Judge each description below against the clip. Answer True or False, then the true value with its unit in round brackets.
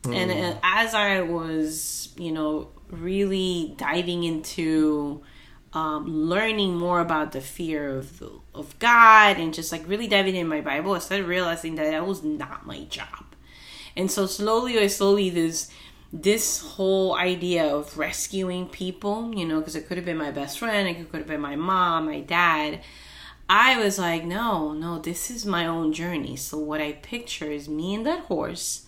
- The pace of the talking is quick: False (175 wpm)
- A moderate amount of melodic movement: True (3.9 semitones)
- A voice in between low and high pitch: True (170 Hz)